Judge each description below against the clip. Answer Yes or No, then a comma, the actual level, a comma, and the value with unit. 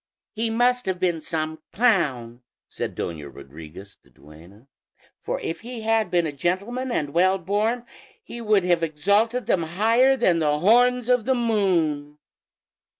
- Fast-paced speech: No, average, 150 wpm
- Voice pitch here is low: No, medium, 185 Hz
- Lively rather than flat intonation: Yes, wide, 7.3 semitones